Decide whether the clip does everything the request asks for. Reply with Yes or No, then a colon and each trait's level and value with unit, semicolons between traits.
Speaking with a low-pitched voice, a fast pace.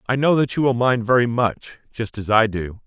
Yes: low, 120 Hz; fast, 250 wpm